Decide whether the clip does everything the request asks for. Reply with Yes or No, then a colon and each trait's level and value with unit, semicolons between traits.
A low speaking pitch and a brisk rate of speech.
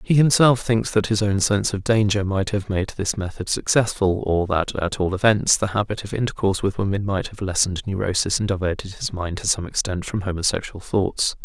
Yes: low, 100 Hz; fast, 210 wpm